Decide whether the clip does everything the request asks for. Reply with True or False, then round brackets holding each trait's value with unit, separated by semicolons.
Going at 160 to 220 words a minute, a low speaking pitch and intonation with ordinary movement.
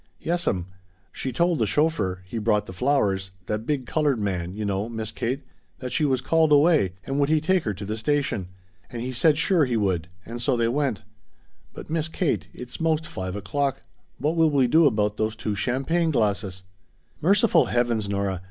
False (190 wpm; 125 Hz; 6.5 semitones)